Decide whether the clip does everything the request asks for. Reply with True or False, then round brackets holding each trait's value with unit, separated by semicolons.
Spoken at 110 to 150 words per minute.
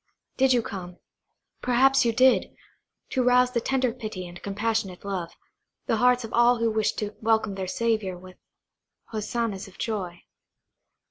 True (140 wpm)